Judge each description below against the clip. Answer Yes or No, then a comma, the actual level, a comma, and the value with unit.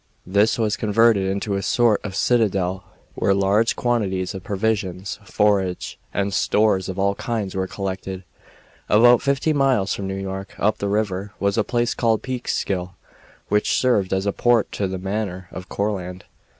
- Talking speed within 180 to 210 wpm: No, average, 165 wpm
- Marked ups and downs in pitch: No, narrow, 2.6 semitones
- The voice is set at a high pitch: No, low, 100 Hz